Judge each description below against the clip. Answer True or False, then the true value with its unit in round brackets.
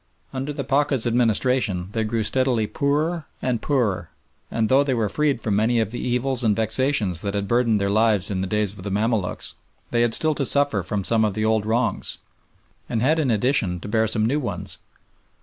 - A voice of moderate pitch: False (115 Hz)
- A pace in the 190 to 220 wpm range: True (205 wpm)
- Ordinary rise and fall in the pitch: True (4.0 semitones)